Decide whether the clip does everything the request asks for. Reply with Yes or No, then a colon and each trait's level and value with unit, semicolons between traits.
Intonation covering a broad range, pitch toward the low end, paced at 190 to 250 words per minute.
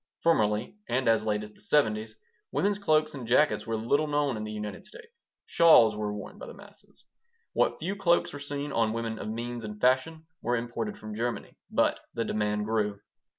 Yes: wide, 6.1 semitones; low, 120 Hz; average, 195 wpm